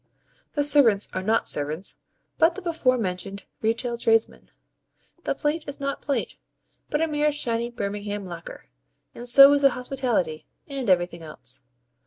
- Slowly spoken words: No, average, 150 wpm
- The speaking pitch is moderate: No, high, 235 Hz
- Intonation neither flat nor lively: No, wide, 6.5 semitones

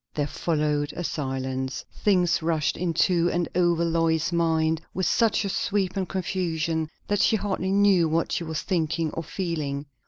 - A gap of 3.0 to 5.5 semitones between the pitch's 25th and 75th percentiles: No, narrow, 2.6 semitones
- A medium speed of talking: Yes, average, 160 wpm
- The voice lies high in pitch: No, medium, 165 Hz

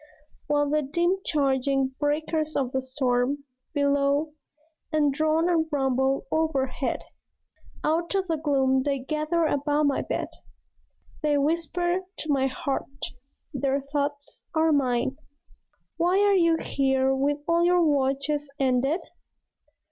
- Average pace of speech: No, slow, 125 wpm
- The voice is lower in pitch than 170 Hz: No, very high, 290 Hz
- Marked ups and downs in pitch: No, average, 2.8 semitones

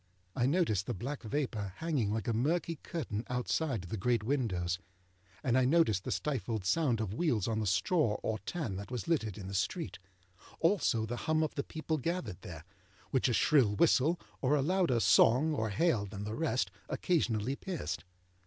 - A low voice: Yes, low, 120 Hz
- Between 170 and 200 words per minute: Yes, average, 180 wpm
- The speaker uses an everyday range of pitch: No, wide, 6.8 semitones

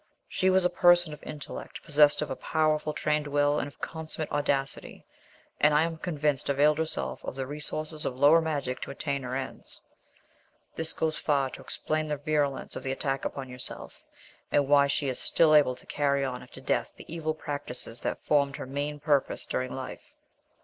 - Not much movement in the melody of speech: Yes, narrow, 2.1 semitones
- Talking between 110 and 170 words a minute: No, average, 190 wpm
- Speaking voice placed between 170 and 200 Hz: No, medium, 145 Hz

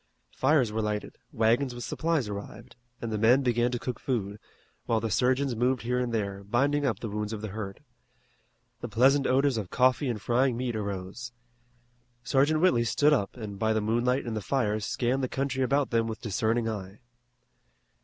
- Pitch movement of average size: Yes, average, 3.3 semitones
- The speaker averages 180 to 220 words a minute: Yes, average, 185 wpm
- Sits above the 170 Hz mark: No, low, 120 Hz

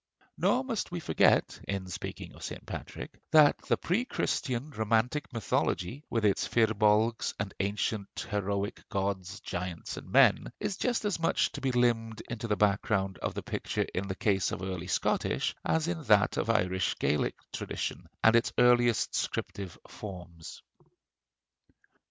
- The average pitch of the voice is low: Yes, low, 110 Hz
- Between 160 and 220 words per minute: No, average, 150 wpm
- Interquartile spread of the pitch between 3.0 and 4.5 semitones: Yes, average, 4.0 semitones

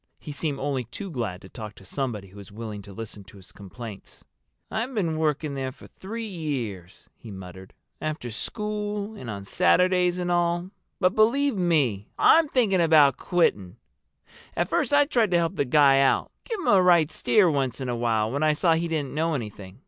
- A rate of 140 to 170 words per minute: No, average, 195 wpm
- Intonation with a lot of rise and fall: Yes, wide, 8.3 semitones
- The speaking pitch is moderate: Yes, medium, 150 Hz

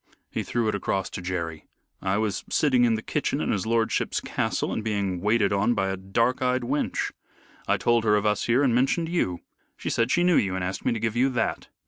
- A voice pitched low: Yes, low, 110 Hz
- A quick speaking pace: Yes, fast, 230 wpm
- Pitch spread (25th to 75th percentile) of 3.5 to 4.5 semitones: Yes, average, 4.2 semitones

